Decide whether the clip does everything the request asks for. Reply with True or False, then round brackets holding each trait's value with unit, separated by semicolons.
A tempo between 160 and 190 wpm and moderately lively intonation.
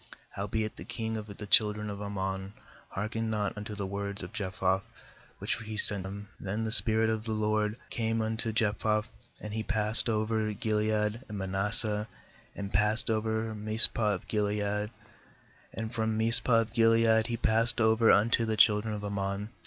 False (175 wpm; 1.3 semitones)